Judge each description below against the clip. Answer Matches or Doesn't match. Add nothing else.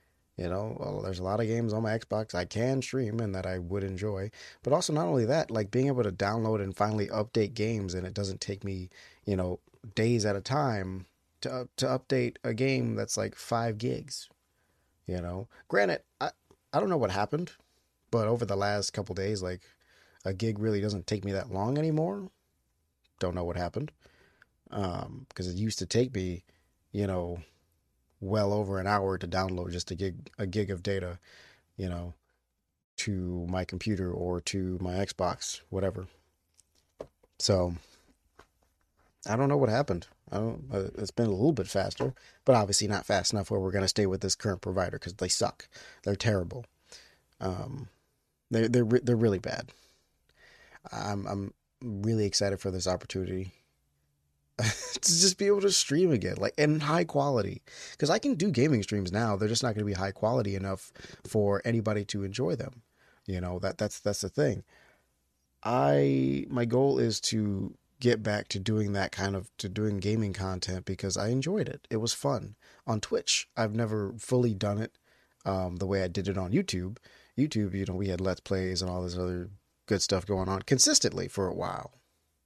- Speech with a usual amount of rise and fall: Matches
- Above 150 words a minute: Matches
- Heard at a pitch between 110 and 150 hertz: Doesn't match